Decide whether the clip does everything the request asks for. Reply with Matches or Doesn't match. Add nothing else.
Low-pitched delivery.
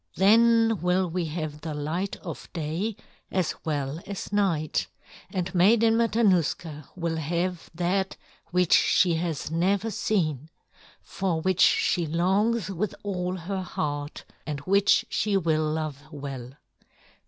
Doesn't match